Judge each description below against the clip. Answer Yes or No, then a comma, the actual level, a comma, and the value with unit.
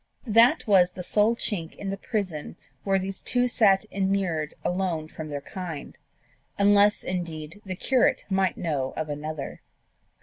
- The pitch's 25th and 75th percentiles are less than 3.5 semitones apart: No, average, 4.3 semitones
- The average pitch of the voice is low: No, high, 190 Hz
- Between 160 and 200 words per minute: No, average, 145 wpm